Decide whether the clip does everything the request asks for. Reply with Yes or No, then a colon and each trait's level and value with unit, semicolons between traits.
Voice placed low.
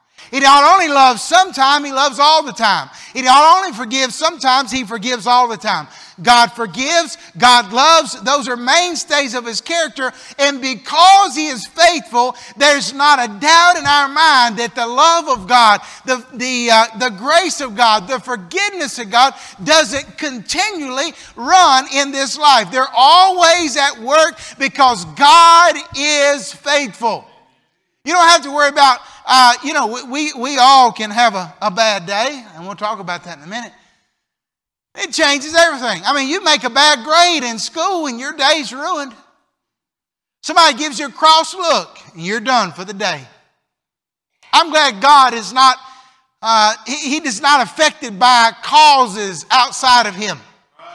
No: very high, 270 Hz